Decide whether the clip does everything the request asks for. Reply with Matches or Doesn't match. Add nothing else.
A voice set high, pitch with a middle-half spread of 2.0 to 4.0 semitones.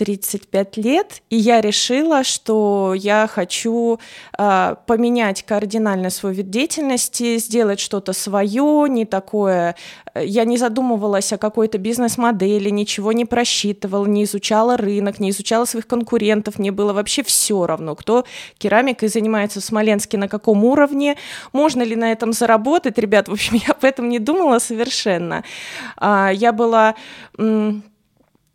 Matches